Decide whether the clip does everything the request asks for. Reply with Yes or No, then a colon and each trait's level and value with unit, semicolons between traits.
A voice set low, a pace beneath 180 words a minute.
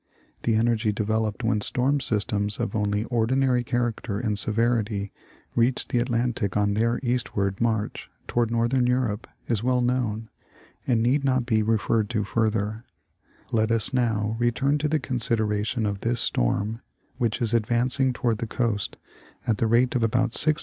Yes: low, 115 Hz; average, 160 wpm